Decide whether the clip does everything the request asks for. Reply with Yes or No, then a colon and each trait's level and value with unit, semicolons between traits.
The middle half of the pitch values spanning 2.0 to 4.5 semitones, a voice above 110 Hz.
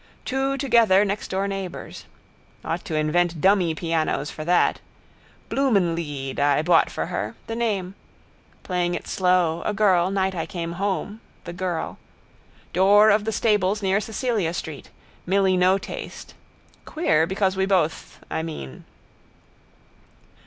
Yes: average, 3.4 semitones; medium, 185 Hz